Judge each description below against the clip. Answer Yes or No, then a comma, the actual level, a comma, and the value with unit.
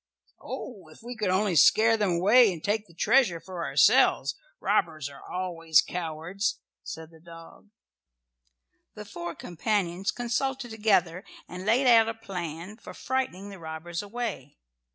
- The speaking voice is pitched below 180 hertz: No, high, 190 Hz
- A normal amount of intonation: Yes, average, 4.7 semitones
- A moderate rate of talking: Yes, average, 145 wpm